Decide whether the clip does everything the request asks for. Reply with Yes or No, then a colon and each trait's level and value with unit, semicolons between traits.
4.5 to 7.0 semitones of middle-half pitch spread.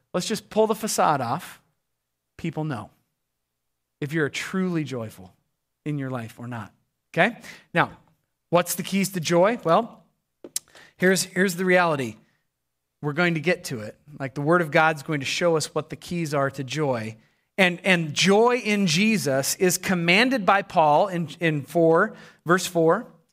Yes: average, 5.2 semitones